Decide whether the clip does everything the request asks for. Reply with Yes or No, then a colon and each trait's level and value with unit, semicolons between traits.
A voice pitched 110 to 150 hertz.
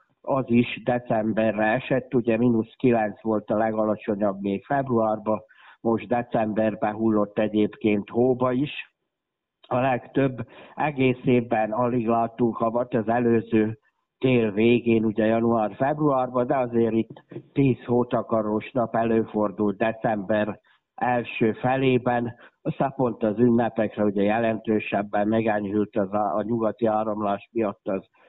Yes: low, 115 Hz